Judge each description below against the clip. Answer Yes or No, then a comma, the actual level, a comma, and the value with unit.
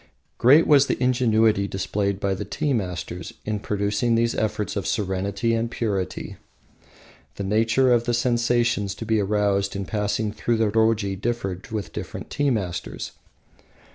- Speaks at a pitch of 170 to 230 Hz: No, low, 110 Hz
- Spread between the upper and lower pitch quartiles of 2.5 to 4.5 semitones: Yes, average, 3.0 semitones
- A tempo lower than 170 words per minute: Yes, average, 150 wpm